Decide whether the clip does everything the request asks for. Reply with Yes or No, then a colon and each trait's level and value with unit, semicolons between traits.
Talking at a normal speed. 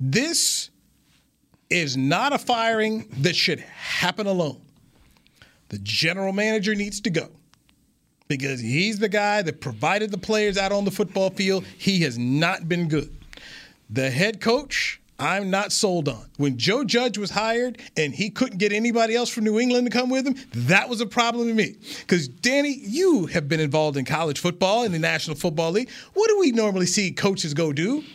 Yes: average, 185 wpm